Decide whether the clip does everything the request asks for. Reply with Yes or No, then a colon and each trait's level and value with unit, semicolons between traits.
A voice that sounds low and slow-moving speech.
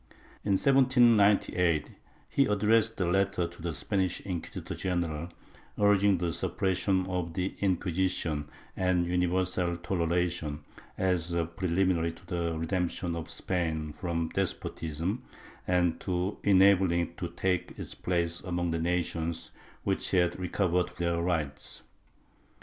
Yes: very low, 90 Hz; slow, 120 wpm